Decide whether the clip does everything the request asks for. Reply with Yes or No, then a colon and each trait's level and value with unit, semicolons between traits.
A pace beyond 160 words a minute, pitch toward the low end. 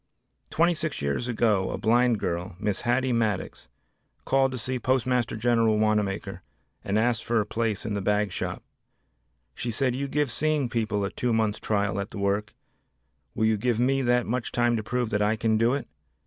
Yes: average, 190 wpm; low, 115 Hz